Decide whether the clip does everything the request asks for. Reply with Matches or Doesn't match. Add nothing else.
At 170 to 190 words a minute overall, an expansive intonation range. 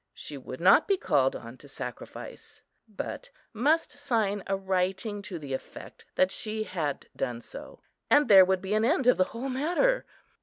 Matches